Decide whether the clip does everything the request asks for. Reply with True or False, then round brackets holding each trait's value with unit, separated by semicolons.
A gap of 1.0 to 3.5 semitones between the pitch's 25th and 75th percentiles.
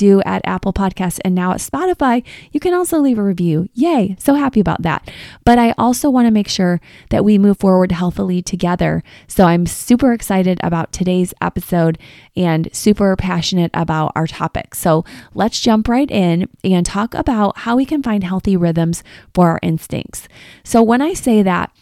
False (5.0 semitones)